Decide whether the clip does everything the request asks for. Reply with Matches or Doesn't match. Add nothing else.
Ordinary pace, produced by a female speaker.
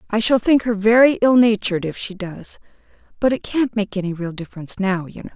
Doesn't match